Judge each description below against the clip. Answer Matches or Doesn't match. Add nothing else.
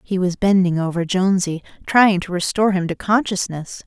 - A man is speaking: Doesn't match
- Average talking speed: Matches